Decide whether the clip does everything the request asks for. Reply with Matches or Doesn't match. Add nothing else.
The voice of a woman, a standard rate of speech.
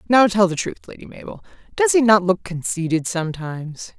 Matches